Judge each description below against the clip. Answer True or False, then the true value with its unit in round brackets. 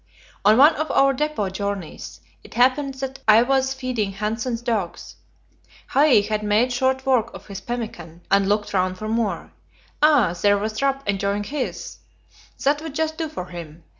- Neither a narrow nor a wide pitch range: True (5.0 semitones)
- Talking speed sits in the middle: True (165 wpm)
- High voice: True (225 Hz)